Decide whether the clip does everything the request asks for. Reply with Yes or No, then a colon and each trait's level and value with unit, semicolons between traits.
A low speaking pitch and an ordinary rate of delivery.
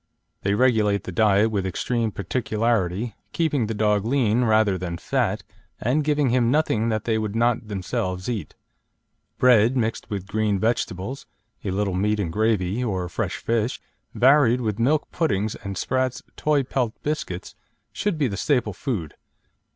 Yes: low, 110 Hz; average, 155 wpm